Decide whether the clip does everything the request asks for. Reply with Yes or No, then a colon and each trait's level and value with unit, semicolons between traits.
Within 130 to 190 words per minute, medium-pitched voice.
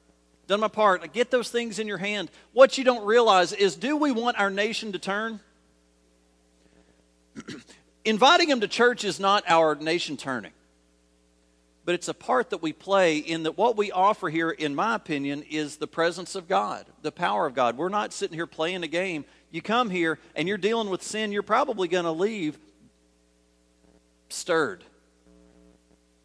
Yes: average, 175 wpm; medium, 170 Hz